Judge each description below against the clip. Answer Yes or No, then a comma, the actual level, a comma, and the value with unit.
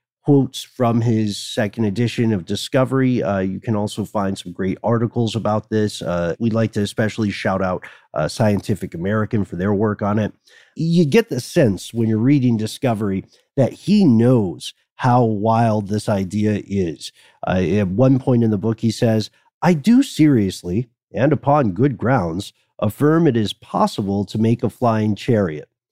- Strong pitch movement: No, average, 3.3 semitones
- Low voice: Yes, low, 110 Hz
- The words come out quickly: No, average, 170 wpm